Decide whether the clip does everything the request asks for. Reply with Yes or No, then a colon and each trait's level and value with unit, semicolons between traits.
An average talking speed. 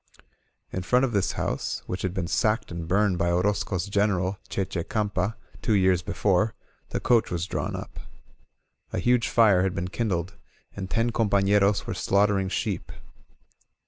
Yes: average, 160 wpm